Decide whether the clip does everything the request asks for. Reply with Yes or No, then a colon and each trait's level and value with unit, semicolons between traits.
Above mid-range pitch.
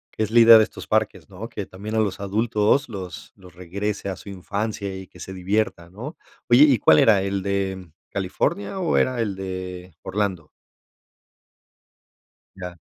No: low, 100 Hz